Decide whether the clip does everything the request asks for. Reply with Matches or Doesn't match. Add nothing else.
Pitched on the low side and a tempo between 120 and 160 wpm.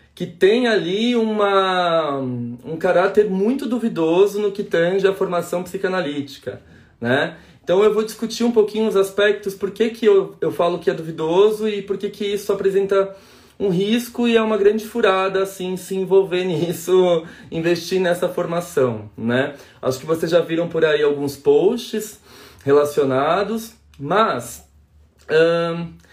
Doesn't match